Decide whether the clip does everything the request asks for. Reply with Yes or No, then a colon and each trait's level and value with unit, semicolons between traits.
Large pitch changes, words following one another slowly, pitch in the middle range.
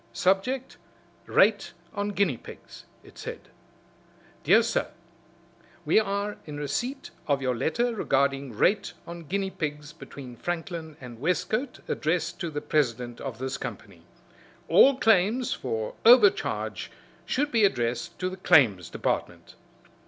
Yes: wide, 6.9 semitones; slow, 130 wpm; medium, 170 Hz